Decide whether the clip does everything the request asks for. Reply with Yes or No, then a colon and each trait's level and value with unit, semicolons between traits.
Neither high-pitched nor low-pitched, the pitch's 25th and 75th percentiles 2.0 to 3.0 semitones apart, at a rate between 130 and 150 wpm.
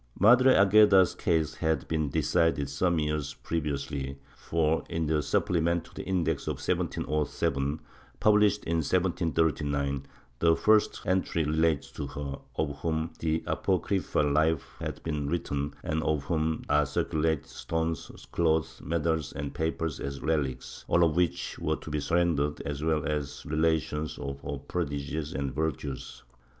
No: very low, 80 Hz; narrow, 2.5 semitones; average, 145 wpm